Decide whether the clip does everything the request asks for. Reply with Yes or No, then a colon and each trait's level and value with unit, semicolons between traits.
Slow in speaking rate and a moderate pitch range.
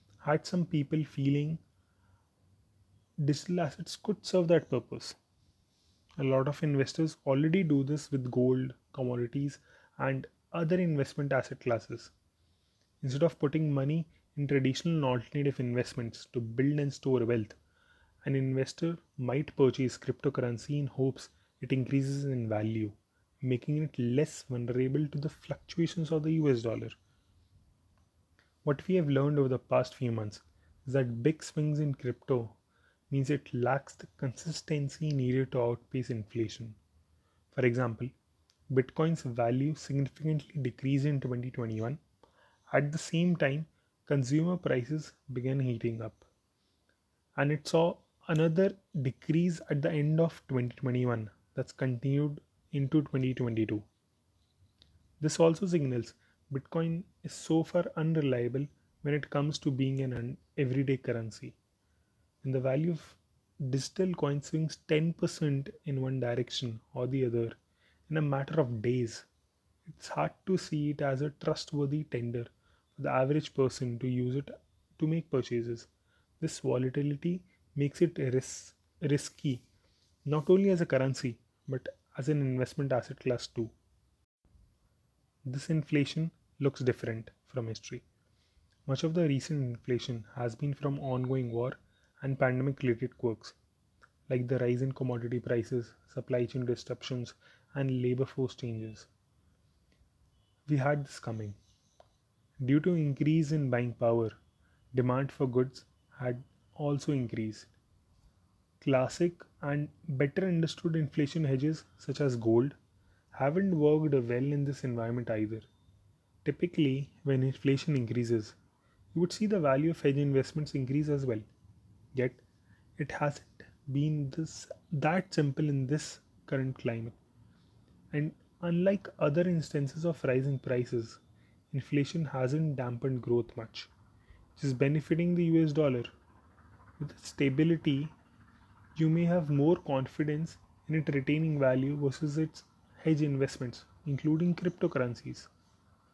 Yes: slow, 130 wpm; average, 4.3 semitones